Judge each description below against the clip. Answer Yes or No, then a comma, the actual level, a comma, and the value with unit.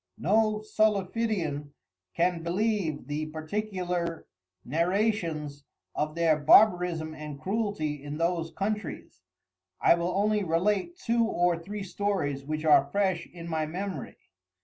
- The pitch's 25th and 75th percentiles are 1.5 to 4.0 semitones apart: No, average, 4.8 semitones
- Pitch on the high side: No, medium, 175 Hz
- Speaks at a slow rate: Yes, slow, 120 wpm